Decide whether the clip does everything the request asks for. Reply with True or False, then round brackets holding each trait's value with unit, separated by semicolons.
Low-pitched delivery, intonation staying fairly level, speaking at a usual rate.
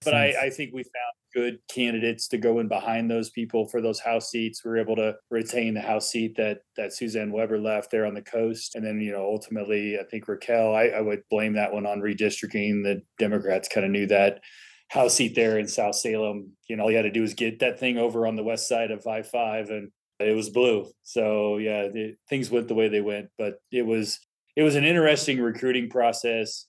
False (110 Hz; 1.7 semitones; 235 wpm)